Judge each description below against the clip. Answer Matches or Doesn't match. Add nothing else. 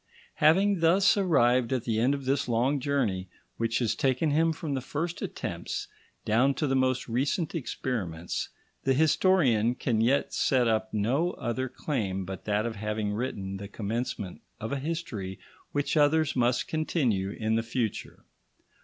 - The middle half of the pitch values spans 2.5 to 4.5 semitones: Doesn't match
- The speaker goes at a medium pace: Matches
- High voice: Doesn't match